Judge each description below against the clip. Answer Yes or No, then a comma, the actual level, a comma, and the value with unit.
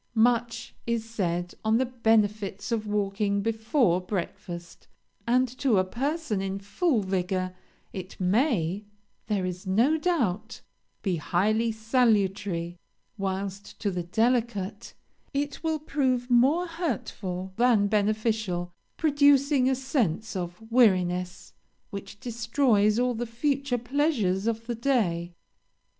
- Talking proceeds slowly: Yes, slow, 120 wpm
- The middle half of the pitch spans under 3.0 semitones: No, average, 4.7 semitones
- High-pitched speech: Yes, high, 220 Hz